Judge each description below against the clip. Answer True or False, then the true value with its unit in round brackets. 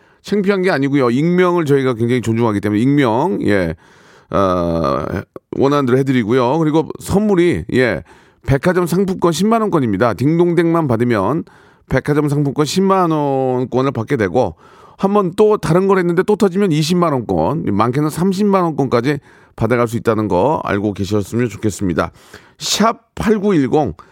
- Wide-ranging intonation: True (7.3 semitones)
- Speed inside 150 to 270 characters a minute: False (305 characters per minute)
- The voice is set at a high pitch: False (145 Hz)